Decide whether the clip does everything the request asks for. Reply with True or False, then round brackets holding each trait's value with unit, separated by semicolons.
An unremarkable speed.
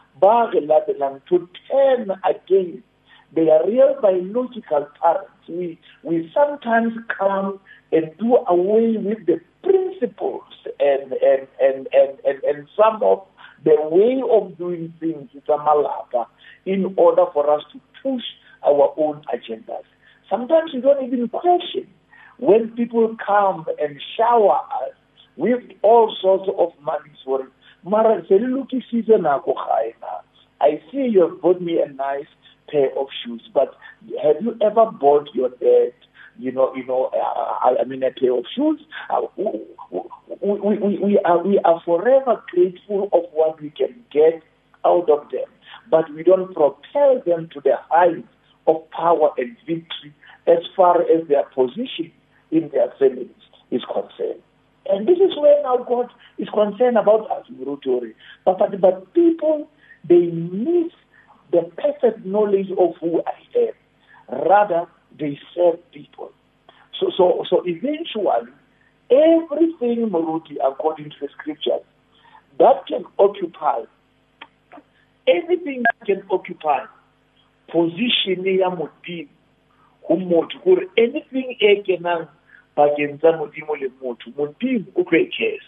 False (130 wpm)